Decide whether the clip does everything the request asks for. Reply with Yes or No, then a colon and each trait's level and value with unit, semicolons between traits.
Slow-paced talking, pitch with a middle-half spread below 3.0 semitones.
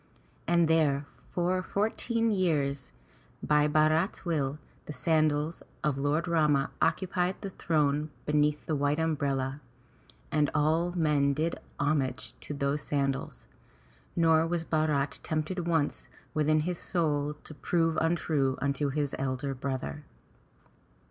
Yes: slow, 120 wpm; narrow, 2.5 semitones